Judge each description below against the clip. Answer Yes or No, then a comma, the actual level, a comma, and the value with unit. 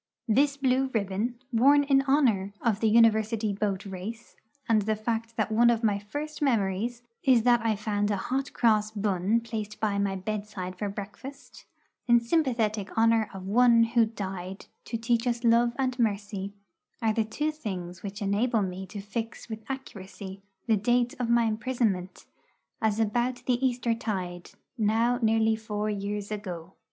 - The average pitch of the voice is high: Yes, high, 220 Hz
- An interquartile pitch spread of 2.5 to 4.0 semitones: Yes, average, 2.9 semitones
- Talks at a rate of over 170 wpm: No, average, 165 wpm